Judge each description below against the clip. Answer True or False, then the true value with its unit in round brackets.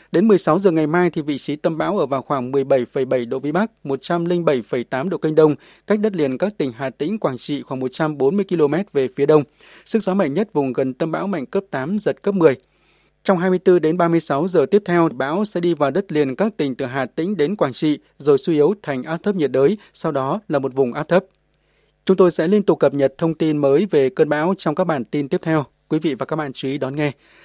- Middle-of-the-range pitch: True (155 Hz)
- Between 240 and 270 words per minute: True (250 wpm)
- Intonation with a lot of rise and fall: False (4.8 semitones)